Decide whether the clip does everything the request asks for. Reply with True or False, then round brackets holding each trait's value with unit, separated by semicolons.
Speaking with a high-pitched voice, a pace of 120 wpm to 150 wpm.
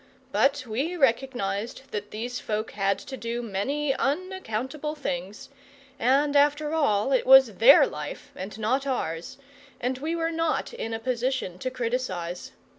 True (255 Hz; 145 wpm)